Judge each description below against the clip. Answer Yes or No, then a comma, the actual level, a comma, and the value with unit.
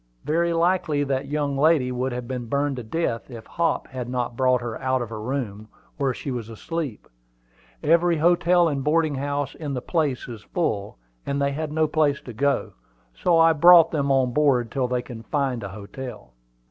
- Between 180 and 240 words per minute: Yes, average, 195 wpm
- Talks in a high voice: No, medium, 140 Hz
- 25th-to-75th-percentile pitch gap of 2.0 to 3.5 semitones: No, average, 4.2 semitones